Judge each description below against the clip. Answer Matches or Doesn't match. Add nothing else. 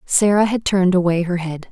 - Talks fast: Matches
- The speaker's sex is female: Matches